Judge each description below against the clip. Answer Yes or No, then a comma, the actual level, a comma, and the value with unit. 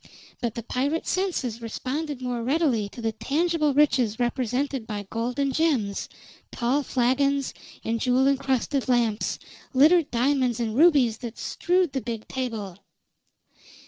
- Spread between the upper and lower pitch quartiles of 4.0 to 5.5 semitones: No, average, 3.6 semitones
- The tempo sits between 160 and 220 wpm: No, slow, 135 wpm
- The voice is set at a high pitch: Yes, very high, 255 Hz